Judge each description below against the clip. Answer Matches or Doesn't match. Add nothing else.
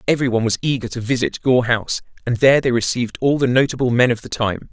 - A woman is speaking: Doesn't match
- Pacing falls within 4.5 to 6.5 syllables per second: Doesn't match